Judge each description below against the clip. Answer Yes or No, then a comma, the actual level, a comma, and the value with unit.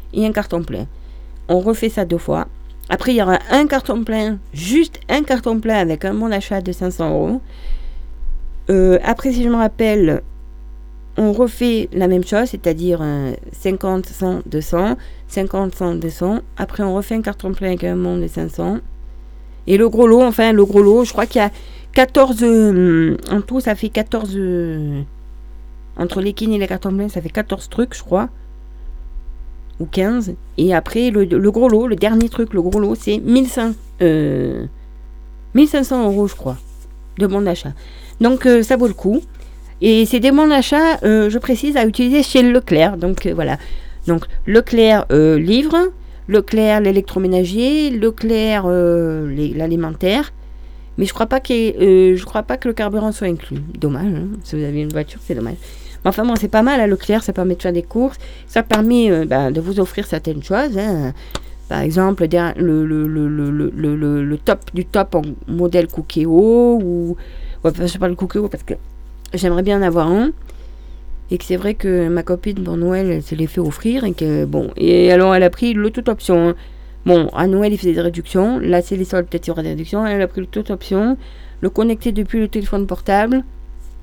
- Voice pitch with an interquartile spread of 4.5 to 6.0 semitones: Yes, average, 5.2 semitones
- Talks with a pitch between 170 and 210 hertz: Yes, high, 190 Hz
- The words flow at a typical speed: Yes, average, 195 wpm